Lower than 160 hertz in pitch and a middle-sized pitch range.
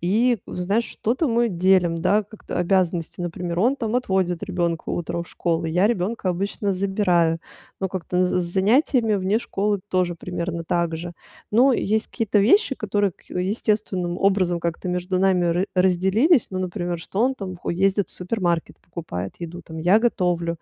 No: medium, 185 Hz; average, 3.2 semitones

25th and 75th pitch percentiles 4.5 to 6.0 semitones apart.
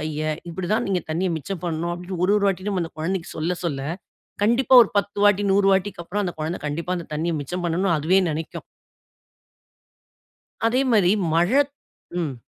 No: average, 3.5 semitones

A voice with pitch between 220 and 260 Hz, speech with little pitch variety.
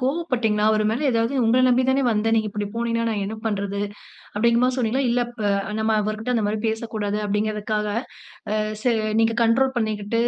Yes: high, 225 Hz; narrow, 2.1 semitones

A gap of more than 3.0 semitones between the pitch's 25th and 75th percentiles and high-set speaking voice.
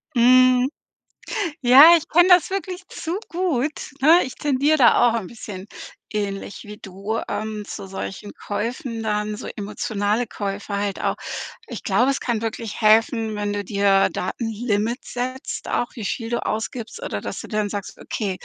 Yes: average, 3.9 semitones; high, 225 Hz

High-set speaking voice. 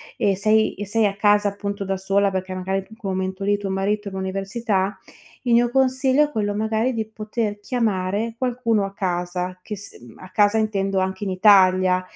Yes: high, 200 Hz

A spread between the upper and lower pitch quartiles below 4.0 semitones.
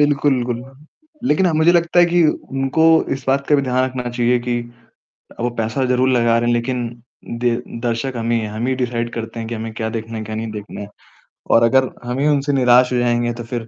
Yes: narrow, 2.4 semitones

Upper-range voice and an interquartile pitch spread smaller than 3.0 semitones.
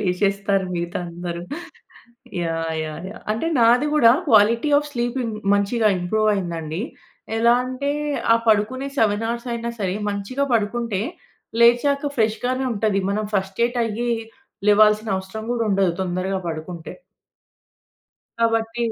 No: high, 215 Hz; average, 3.7 semitones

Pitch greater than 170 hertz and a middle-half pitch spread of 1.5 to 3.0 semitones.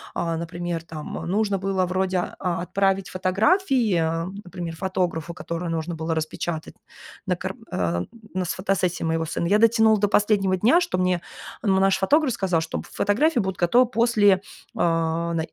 No: medium, 185 Hz; average, 3.4 semitones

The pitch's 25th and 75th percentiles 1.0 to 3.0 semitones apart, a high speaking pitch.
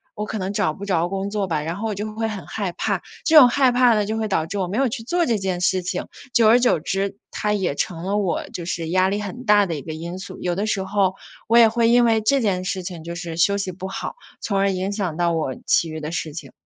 No: average, 3.7 semitones; high, 195 Hz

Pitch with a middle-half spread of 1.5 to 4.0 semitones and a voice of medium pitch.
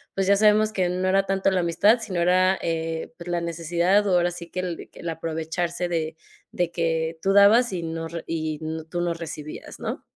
Yes: narrow, 2.5 semitones; medium, 175 Hz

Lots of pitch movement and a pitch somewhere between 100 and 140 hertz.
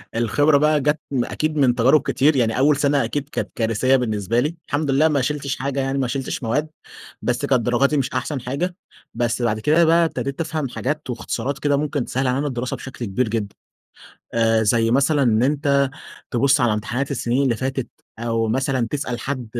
No: average, 3.3 semitones; low, 135 Hz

